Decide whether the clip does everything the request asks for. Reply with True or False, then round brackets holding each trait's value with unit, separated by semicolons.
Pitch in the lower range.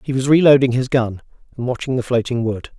True (125 Hz)